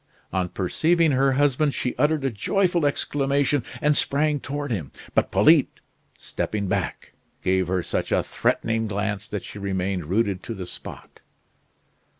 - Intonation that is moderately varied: No, wide, 6.9 semitones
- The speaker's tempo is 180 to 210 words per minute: No, average, 150 wpm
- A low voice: Yes, low, 115 Hz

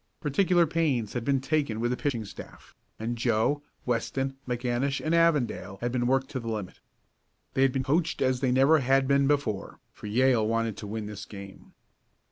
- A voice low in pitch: Yes, low, 130 Hz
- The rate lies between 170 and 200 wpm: Yes, average, 185 wpm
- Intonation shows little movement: No, average, 3.4 semitones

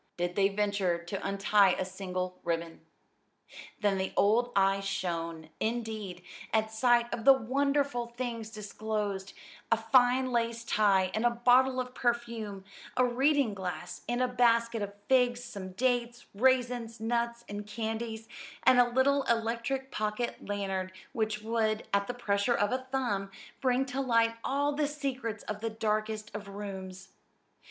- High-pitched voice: Yes, high, 225 Hz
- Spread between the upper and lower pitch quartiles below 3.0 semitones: No, average, 3.4 semitones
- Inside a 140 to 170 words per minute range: Yes, average, 150 wpm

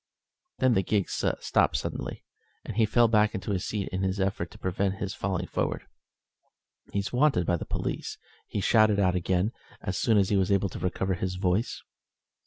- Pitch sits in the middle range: No, very low, 95 Hz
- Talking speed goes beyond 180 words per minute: Yes, average, 190 wpm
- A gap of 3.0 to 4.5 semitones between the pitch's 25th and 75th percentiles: No, narrow, 2.4 semitones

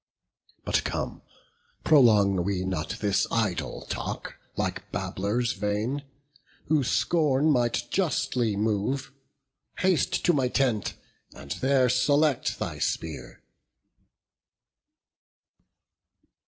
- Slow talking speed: Yes, slow, 90 wpm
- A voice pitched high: No, low, 120 Hz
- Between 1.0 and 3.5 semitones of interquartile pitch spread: No, wide, 5.4 semitones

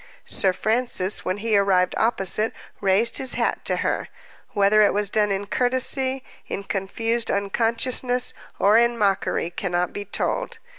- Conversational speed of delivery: Yes, average, 145 wpm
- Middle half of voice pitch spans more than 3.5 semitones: No, average, 3.2 semitones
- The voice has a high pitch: Yes, high, 210 Hz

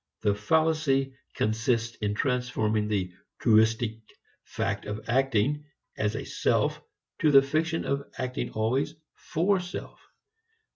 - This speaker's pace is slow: Yes, slow, 115 wpm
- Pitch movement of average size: Yes, average, 4.9 semitones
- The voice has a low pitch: Yes, low, 125 Hz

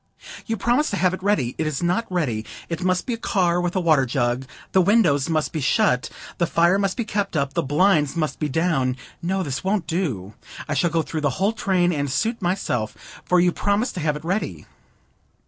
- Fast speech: Yes, fast, 215 wpm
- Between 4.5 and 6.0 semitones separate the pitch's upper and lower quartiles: Yes, average, 4.9 semitones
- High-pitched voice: No, medium, 170 Hz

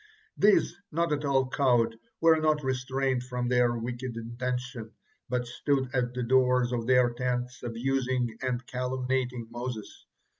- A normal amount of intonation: No, narrow, 1.4 semitones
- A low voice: Yes, low, 125 Hz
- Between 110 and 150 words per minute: Yes, average, 140 wpm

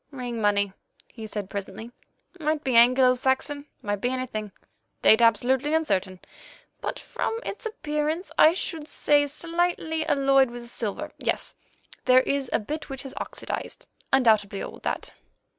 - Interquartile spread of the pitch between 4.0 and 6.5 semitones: Yes, average, 5.1 semitones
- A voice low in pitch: No, very high, 260 Hz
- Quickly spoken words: No, average, 140 wpm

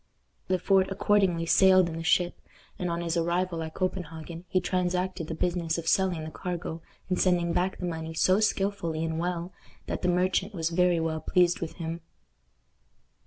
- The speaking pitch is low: No, medium, 175 Hz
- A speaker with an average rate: Yes, average, 175 wpm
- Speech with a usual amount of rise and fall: No, narrow, 2.0 semitones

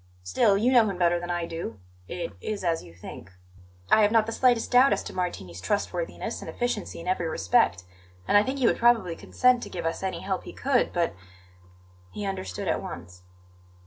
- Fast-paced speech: Yes, fast, 210 wpm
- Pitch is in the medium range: Yes, medium, 180 Hz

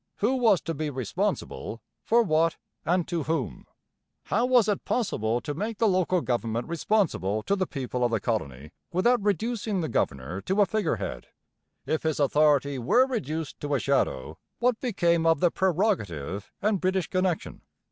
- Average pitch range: No, wide, 8.2 semitones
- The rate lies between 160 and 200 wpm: Yes, average, 165 wpm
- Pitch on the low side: No, medium, 165 Hz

